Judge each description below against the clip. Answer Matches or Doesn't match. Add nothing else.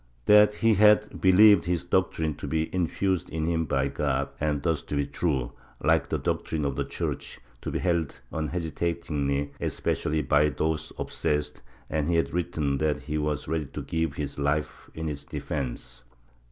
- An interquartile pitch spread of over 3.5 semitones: Doesn't match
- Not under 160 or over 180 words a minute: Matches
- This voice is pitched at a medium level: Doesn't match